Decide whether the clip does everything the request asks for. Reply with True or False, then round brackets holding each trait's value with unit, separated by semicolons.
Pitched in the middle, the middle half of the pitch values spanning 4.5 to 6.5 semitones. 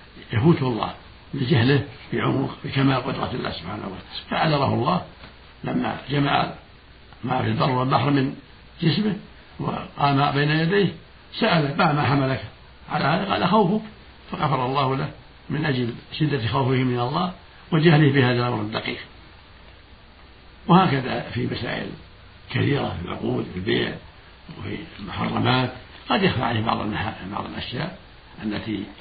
False (130 Hz; 5.3 semitones)